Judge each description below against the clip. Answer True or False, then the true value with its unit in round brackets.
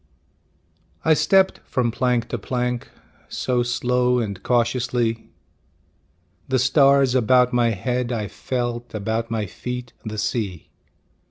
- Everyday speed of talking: False (115 wpm)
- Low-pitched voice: True (120 Hz)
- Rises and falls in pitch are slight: True (1.7 semitones)